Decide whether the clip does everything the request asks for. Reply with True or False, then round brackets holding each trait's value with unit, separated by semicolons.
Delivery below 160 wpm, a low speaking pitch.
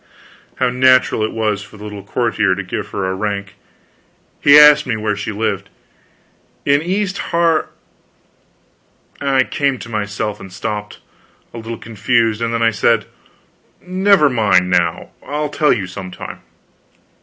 True (150 wpm; 110 Hz)